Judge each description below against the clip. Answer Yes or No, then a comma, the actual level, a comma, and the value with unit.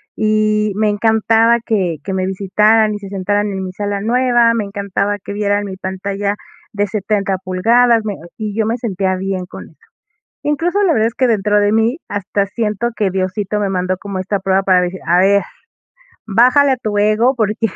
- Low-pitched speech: No, high, 205 Hz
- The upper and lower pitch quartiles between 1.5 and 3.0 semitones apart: Yes, narrow, 2.4 semitones